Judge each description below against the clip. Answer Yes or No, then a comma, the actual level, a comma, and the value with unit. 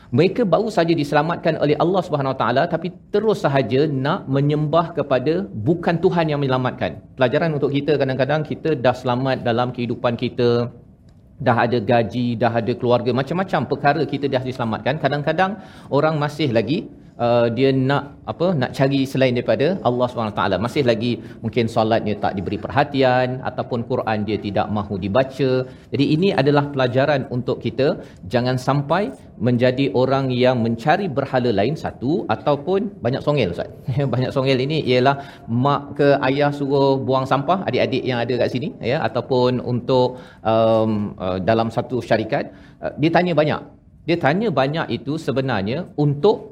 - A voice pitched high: No, low, 130 Hz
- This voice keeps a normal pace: No, fast, 155 wpm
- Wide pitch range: No, average, 3.5 semitones